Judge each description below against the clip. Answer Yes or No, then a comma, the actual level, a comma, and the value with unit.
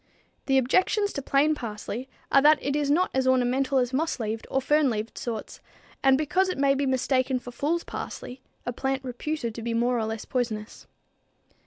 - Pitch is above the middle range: Yes, very high, 265 Hz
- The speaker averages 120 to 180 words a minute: No, average, 190 wpm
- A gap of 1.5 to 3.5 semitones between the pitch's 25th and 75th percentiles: Yes, average, 2.8 semitones